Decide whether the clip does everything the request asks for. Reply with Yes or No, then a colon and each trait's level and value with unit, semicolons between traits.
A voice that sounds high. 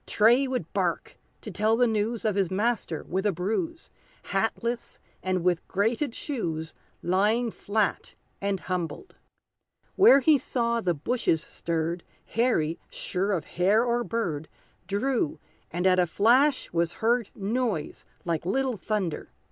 Yes: high, 210 Hz